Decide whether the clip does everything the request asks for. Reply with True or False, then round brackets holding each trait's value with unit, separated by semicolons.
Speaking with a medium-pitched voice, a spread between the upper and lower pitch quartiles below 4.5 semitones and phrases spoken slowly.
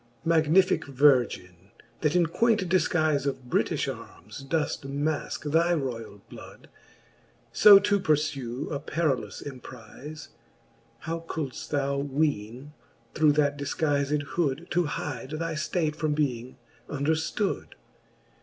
True (150 Hz; 2.9 semitones; 115 wpm)